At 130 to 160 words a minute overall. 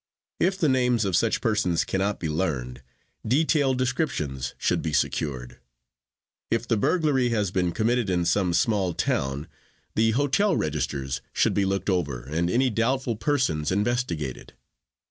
Yes: average, 145 wpm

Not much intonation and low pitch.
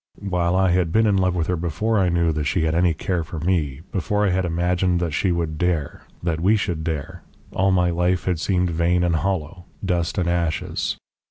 Yes: narrow, 2.0 semitones; very low, 90 Hz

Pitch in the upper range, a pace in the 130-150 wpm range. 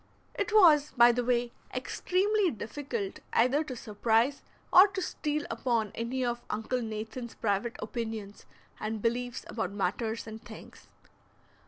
Yes: high, 235 Hz; slow, 135 wpm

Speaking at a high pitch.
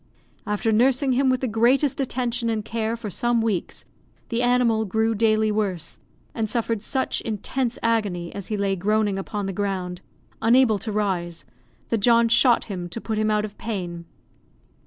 Yes: high, 220 Hz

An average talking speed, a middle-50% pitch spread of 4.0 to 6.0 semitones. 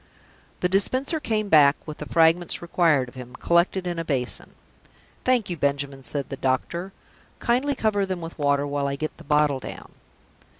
Yes: average, 175 wpm; average, 5.1 semitones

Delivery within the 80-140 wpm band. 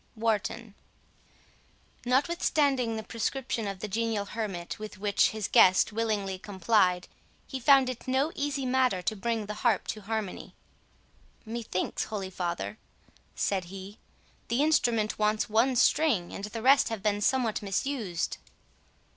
Yes: slow, 135 wpm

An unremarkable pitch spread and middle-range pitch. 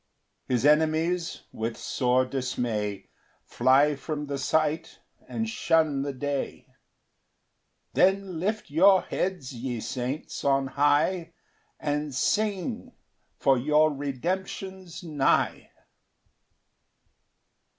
Yes: average, 4.5 semitones; medium, 150 Hz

